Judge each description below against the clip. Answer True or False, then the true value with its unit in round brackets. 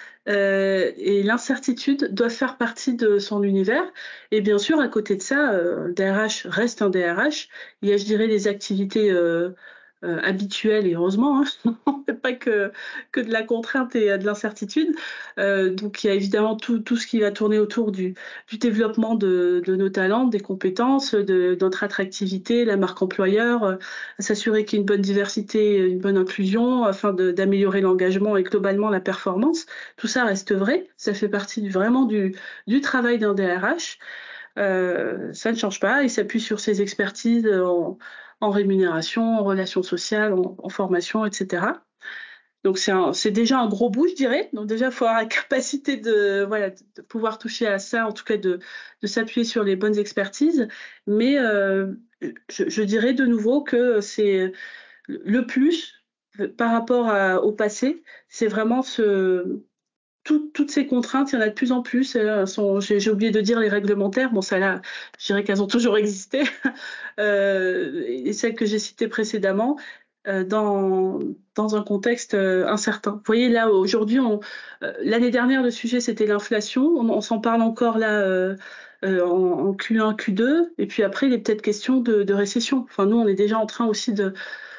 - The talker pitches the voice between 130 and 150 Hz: False (215 Hz)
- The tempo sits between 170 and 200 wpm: True (190 wpm)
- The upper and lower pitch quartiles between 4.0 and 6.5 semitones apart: False (3.6 semitones)